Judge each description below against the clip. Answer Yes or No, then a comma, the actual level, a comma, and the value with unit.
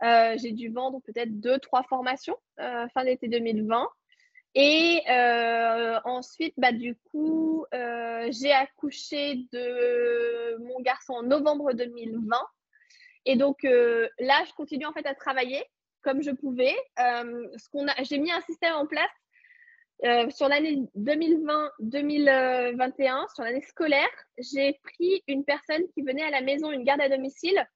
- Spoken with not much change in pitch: No, average, 3.8 semitones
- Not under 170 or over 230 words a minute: No, average, 155 wpm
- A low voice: No, very high, 270 Hz